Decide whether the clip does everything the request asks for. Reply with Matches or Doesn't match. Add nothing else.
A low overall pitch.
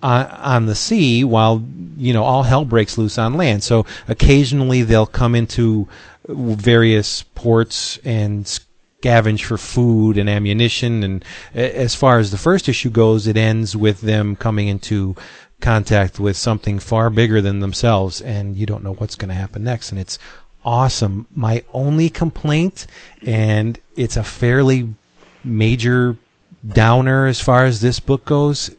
Matches